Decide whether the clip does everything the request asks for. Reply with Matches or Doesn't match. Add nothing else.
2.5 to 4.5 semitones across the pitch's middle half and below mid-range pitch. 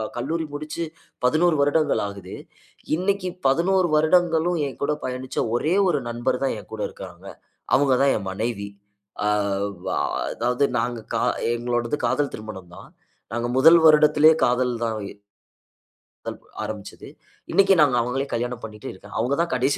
Doesn't match